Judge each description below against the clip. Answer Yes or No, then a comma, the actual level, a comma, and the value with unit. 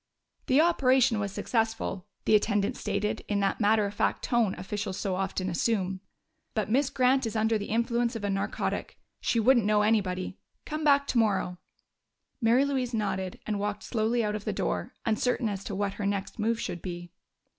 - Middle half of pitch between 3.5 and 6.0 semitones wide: No, average, 3.0 semitones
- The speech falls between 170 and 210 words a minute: Yes, average, 180 wpm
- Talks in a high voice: Yes, high, 215 Hz